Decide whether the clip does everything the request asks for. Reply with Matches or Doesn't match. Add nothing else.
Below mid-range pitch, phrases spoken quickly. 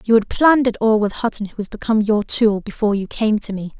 Doesn't match